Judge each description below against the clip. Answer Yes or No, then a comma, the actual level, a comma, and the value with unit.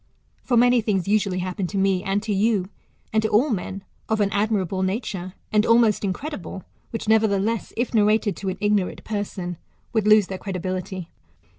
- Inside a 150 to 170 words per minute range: No, average, 180 wpm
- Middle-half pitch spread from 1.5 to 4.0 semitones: Yes, narrow, 2.5 semitones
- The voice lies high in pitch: Yes, high, 205 Hz